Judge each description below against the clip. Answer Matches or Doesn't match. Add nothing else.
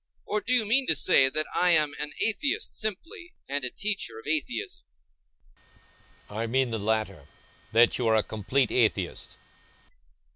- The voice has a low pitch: Matches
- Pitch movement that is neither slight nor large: Doesn't match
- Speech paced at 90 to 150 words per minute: Matches